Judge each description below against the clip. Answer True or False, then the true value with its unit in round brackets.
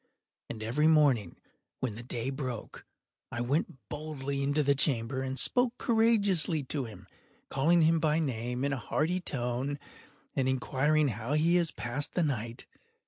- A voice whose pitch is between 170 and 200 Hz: False (140 Hz)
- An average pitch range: True (4.1 semitones)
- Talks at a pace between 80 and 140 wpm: False (155 wpm)